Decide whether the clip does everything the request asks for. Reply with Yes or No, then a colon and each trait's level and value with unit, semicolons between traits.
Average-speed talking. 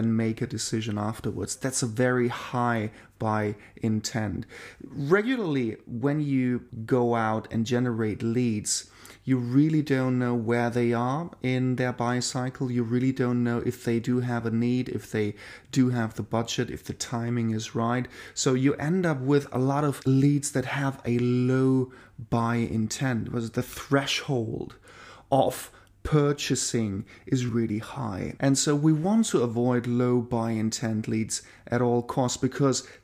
Yes: average, 160 wpm